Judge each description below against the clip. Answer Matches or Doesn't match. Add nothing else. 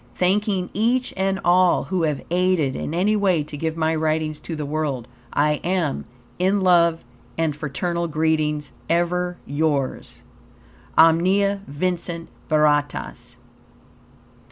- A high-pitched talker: Doesn't match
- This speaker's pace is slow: Matches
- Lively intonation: Doesn't match